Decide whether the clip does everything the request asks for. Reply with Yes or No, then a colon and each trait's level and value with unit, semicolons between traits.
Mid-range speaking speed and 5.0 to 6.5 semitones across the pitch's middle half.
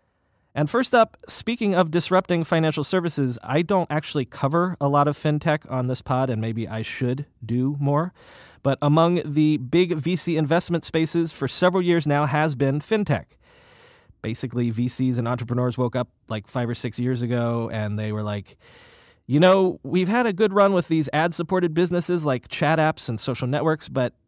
Yes: average, 185 wpm; wide, 5.6 semitones